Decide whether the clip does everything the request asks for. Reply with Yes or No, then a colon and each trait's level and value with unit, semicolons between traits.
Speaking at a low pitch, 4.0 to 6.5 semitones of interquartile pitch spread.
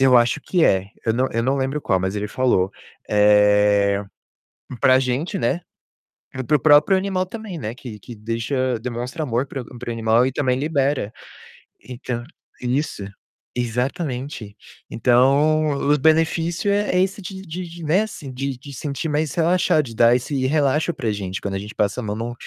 Yes: low, 130 Hz; average, 5.1 semitones